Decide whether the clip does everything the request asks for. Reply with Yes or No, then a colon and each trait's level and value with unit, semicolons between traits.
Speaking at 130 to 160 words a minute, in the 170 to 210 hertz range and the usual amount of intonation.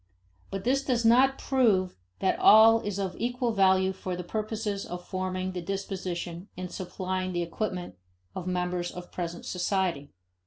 Yes: average, 155 wpm; medium, 185 Hz; average, 3.2 semitones